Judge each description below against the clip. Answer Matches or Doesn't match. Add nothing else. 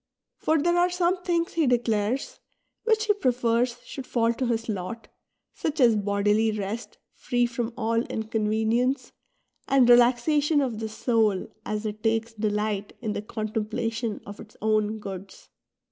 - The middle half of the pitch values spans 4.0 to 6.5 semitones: Doesn't match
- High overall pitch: Matches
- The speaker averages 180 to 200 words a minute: Doesn't match